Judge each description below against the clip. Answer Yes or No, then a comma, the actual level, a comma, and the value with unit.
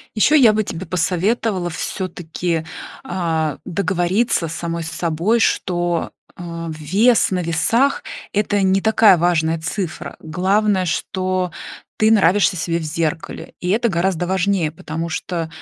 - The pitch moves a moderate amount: Yes, average, 3.3 semitones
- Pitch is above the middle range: No, medium, 180 Hz